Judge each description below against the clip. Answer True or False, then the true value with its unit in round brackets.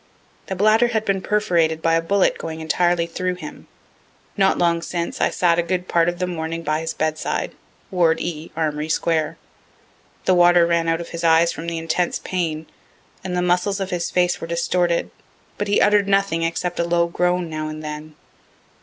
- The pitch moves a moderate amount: False (1.7 semitones)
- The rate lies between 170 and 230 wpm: True (190 wpm)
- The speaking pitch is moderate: True (170 Hz)